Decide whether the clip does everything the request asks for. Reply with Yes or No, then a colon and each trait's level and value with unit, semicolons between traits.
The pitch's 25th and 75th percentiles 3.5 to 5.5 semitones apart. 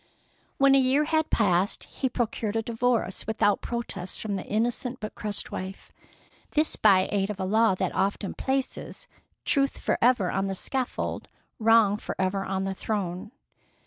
Yes: average, 4.2 semitones